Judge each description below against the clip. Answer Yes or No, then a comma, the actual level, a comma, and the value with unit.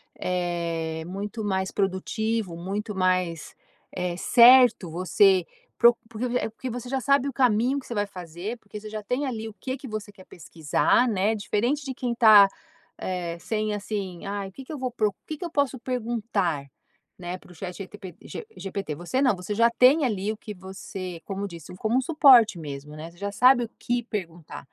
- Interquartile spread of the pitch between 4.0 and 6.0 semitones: Yes, average, 4.8 semitones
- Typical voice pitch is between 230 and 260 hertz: No, high, 205 Hz